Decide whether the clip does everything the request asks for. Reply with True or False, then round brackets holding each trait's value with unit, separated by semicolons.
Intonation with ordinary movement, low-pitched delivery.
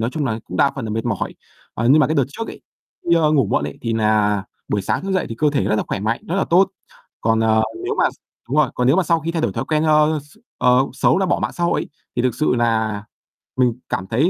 False (5.8 semitones; 130 Hz)